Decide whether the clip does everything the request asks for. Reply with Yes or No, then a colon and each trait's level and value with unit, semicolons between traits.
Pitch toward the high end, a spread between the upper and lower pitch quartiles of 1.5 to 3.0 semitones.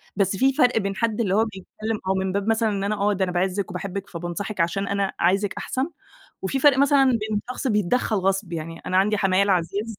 Yes: high, 200 Hz; narrow, 2.6 semitones